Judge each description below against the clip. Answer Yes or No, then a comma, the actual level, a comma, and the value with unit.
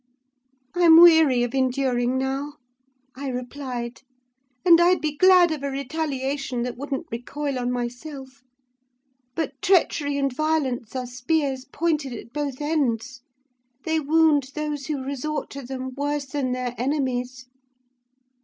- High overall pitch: Yes, very high, 275 Hz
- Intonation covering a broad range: No, average, 3.2 semitones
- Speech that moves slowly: Yes, slow, 130 wpm